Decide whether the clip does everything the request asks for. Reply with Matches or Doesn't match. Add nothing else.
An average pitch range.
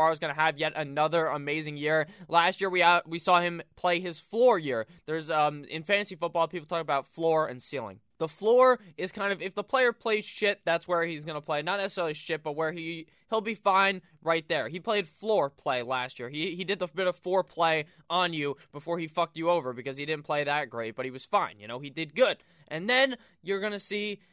Matches